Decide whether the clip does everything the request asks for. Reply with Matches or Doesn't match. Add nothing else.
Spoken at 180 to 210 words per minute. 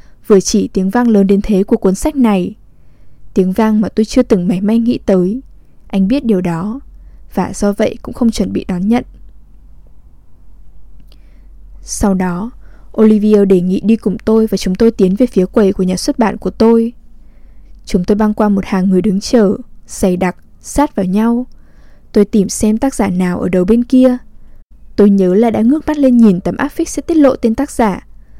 Matches